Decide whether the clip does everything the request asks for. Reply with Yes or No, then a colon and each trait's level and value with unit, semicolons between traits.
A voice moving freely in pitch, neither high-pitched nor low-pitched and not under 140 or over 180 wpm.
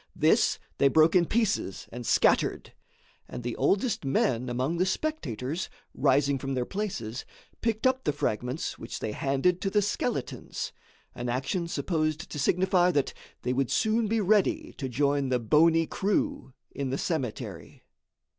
Yes: wide, 7.1 semitones; medium, 150 Hz; average, 155 wpm